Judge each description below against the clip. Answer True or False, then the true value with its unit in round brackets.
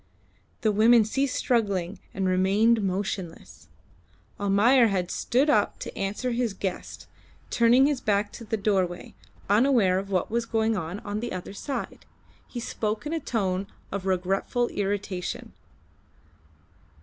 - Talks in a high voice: True (205 Hz)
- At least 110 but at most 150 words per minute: True (135 wpm)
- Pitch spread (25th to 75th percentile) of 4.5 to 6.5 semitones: False (3.5 semitones)